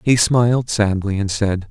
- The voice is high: No, low, 105 Hz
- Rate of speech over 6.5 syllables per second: No, 4.4 syllables/s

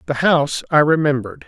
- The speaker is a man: Yes, male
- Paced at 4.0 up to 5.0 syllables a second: No, 6.5 syllables/s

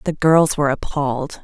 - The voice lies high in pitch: No, medium, 145 Hz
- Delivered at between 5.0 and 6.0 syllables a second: Yes, 5.3 syllables/s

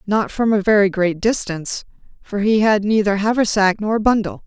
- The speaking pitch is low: No, high, 205 Hz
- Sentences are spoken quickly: No, average, 175 wpm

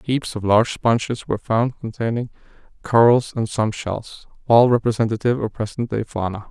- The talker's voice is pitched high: No, low, 115 Hz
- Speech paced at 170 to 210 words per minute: No, average, 155 wpm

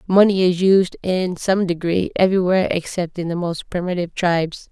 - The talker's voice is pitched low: No, medium, 180 Hz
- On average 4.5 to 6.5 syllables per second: Yes, 5.4 syllables/s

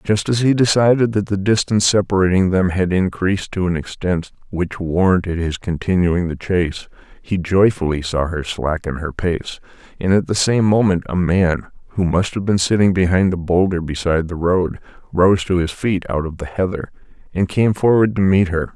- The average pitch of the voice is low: Yes, very low, 90 Hz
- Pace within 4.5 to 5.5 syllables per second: Yes, 5.1 syllables/s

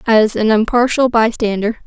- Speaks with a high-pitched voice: Yes, high, 225 Hz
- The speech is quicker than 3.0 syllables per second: Yes, 4.8 syllables/s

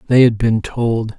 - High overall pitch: No, low, 115 Hz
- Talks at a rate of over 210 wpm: No, fast, 205 wpm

